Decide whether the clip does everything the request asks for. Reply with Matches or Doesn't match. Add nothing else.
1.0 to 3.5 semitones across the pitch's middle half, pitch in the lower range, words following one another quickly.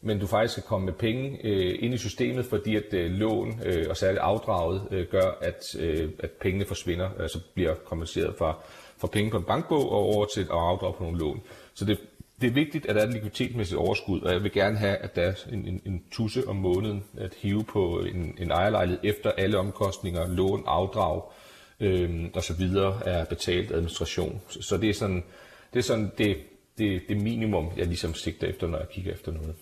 Doesn't match